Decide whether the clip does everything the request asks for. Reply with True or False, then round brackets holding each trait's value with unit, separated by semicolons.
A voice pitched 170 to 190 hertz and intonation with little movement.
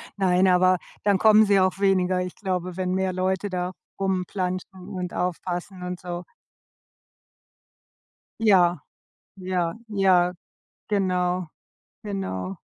True (185 Hz; 1.1 semitones)